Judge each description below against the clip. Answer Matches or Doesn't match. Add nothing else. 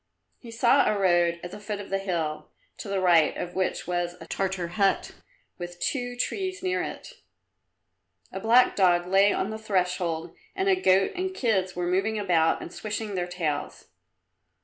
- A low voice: Doesn't match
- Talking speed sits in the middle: Matches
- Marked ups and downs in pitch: Doesn't match